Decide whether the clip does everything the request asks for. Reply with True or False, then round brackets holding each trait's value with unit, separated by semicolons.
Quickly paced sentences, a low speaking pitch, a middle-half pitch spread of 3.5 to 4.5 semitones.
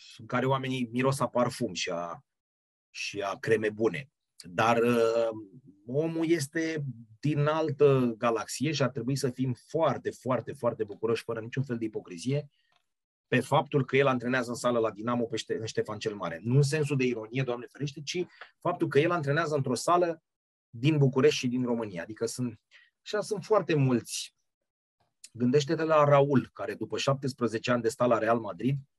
True (175 wpm; 130 Hz; 4.1 semitones)